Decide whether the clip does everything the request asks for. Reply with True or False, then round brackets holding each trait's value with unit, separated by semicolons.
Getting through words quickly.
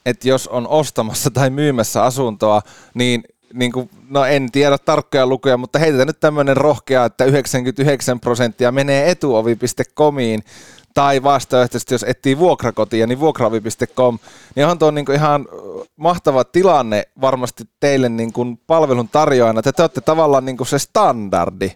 False (145 wpm)